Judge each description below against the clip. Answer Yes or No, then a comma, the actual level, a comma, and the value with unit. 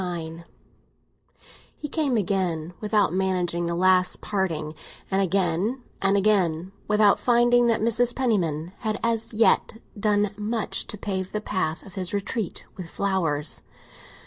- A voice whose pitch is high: Yes, high, 195 Hz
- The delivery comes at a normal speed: No, slow, 130 wpm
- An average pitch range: Yes, average, 3.7 semitones